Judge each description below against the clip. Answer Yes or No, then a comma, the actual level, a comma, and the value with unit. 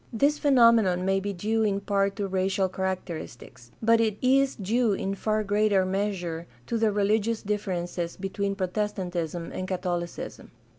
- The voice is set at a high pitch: Yes, high, 200 Hz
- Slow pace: No, average, 145 wpm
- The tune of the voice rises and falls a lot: No, average, 2.7 semitones